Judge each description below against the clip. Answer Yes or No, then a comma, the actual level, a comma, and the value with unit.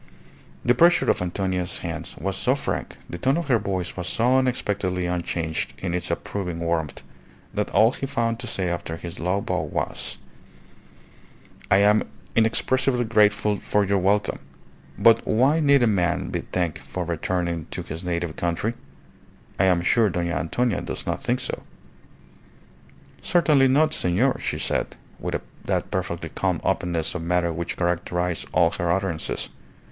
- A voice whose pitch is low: Yes, very low, 95 Hz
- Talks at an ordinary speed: Yes, average, 155 wpm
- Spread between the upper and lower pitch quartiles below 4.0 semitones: No, average, 5.2 semitones